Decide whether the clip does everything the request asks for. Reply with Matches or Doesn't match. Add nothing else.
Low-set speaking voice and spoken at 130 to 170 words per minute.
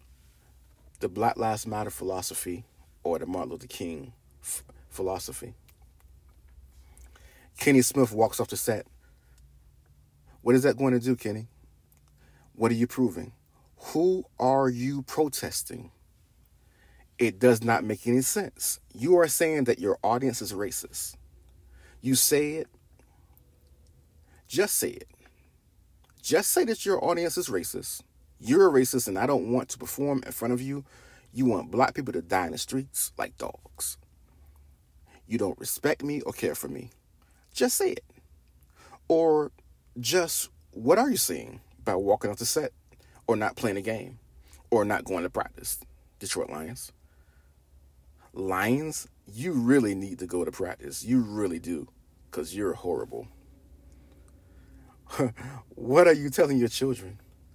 Matches